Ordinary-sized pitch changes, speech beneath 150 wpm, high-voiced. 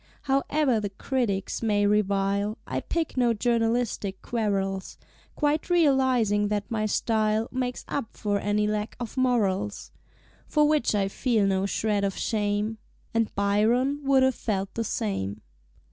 Yes: average, 3.5 semitones; average, 140 wpm; high, 215 Hz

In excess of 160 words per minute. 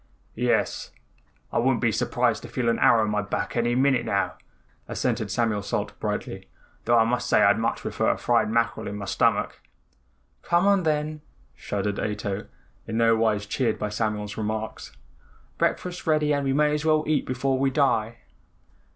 Yes: average, 175 wpm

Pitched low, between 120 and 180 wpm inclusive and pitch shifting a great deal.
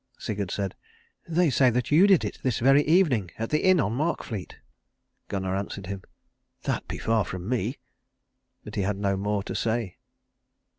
Yes: low, 110 Hz; average, 170 wpm; wide, 5.9 semitones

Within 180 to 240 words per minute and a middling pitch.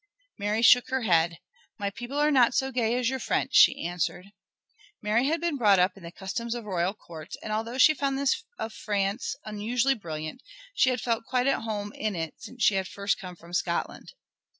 No: fast, 205 wpm; high, 215 Hz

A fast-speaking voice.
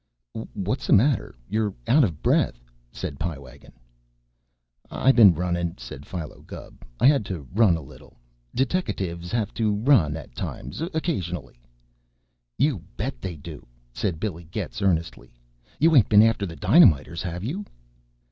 No: average, 145 wpm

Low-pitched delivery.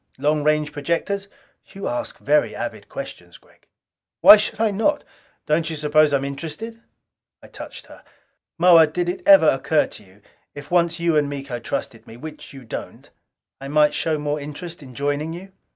No: medium, 155 Hz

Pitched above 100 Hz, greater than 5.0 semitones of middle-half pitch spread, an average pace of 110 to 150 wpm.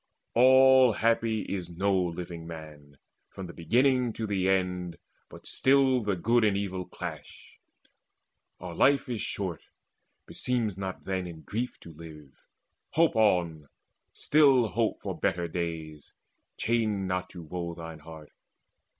No: very low, 95 Hz; wide, 5.5 semitones; slow, 135 wpm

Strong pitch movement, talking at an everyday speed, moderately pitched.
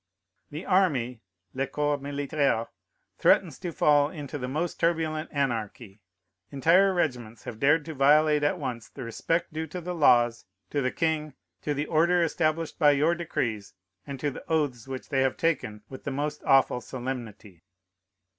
No: average, 3.9 semitones; average, 165 wpm; medium, 145 Hz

